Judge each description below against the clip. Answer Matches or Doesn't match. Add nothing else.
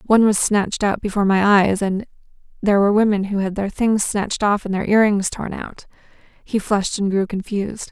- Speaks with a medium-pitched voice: Doesn't match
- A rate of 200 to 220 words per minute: Matches